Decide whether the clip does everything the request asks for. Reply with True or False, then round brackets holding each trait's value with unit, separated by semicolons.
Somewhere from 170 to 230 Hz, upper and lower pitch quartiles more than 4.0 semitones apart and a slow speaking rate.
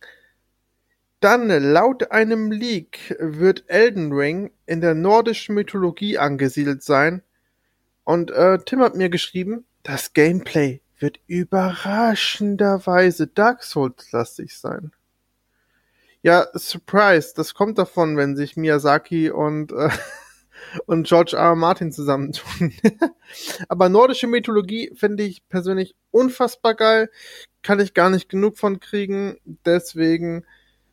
True (185 Hz; 4.8 semitones; 115 wpm)